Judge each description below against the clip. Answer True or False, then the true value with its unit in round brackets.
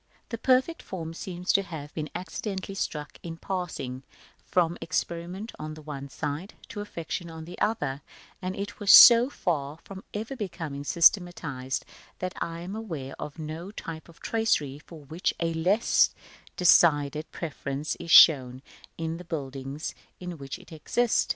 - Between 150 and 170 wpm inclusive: True (155 wpm)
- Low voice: False (165 Hz)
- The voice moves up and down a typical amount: True (4.1 semitones)